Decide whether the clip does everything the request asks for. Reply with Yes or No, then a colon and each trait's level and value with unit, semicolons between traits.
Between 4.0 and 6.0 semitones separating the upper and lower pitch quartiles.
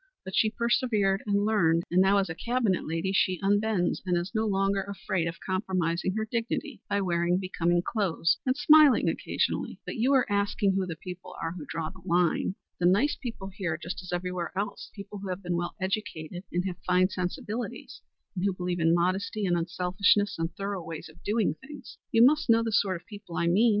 No: average, 2.9 semitones